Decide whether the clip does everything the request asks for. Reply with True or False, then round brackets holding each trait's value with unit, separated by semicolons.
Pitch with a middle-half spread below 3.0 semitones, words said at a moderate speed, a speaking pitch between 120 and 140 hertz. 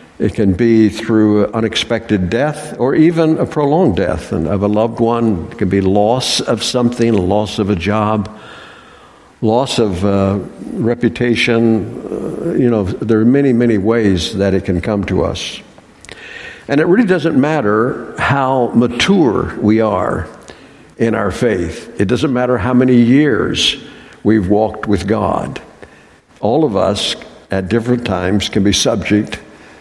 False (2.6 semitones; 150 wpm; 110 Hz)